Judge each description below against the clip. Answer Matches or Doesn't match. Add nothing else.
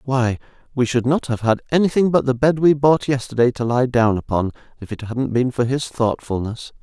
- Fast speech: Matches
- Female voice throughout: Doesn't match